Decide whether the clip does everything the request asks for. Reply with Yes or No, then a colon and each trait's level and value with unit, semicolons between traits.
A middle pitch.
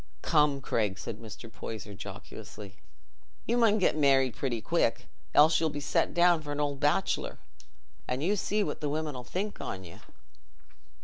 Yes: medium, 145 Hz